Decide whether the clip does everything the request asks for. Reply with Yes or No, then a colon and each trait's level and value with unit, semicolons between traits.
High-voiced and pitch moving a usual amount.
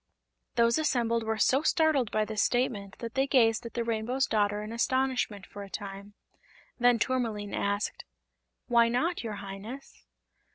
Yes: high, 230 Hz; average, 3.3 semitones